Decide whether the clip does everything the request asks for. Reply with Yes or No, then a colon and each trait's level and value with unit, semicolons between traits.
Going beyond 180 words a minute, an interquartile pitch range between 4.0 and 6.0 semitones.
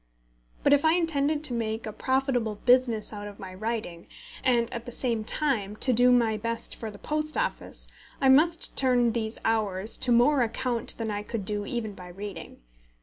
No: average, 190 wpm; average, 3.5 semitones